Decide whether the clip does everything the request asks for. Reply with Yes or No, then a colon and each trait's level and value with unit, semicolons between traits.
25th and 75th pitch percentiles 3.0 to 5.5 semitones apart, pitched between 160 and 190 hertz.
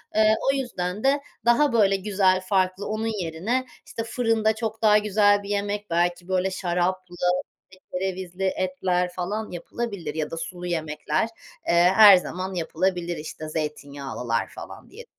Yes: average, 3.3 semitones; medium, 185 Hz